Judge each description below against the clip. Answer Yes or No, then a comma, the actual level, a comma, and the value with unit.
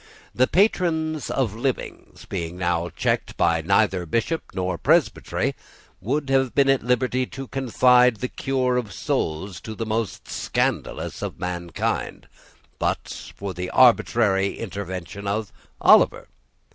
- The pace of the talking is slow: Yes, slow, 130 wpm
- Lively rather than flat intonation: Yes, wide, 5.7 semitones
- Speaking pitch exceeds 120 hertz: No, low, 110 Hz